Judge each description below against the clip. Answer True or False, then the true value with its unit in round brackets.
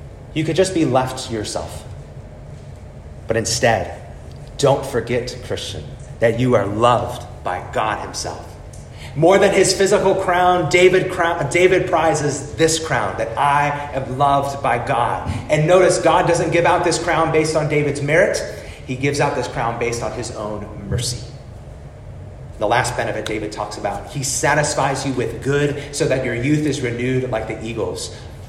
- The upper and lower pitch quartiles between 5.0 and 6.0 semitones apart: True (5.5 semitones)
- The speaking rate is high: False (165 wpm)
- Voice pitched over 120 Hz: True (135 Hz)